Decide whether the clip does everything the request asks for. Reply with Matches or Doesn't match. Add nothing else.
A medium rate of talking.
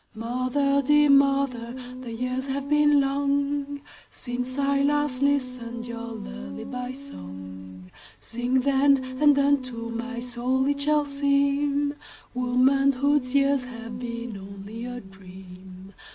Doesn't match